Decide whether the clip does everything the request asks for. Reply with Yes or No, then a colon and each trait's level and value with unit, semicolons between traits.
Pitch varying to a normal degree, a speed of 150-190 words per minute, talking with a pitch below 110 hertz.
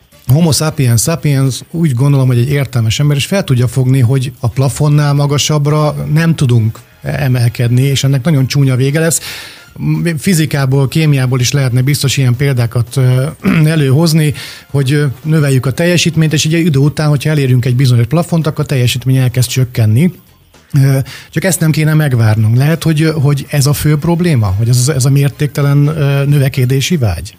No: average, 3.2 semitones; fast, 155 wpm; medium, 140 Hz